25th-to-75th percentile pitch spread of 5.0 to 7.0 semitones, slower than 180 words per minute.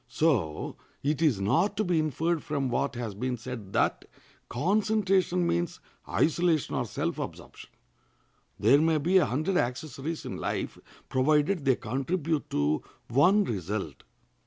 Yes: wide, 5.6 semitones; slow, 135 wpm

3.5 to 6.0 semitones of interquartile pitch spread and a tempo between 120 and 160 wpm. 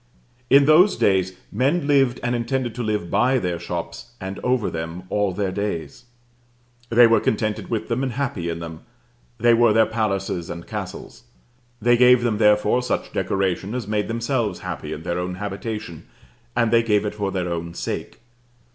No: average, 4.4 semitones; average, 175 wpm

